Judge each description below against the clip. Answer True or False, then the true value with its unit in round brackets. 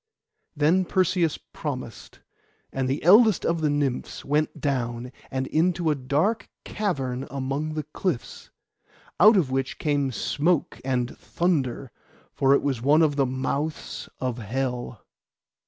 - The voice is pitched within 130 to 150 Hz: True (140 Hz)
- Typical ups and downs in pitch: True (3.7 semitones)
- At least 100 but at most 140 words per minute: True (135 wpm)